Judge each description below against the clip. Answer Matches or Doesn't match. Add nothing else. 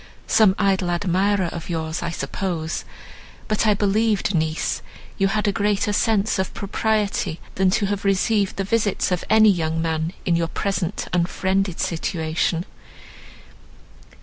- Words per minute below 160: Matches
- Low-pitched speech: Doesn't match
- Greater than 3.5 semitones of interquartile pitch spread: Doesn't match